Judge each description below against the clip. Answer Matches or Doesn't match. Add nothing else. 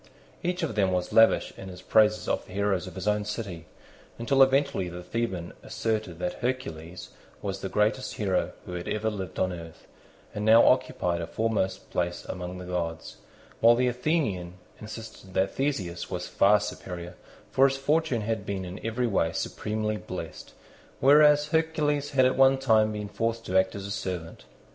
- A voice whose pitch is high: Doesn't match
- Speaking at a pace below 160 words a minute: Doesn't match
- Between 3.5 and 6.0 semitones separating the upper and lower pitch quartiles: Matches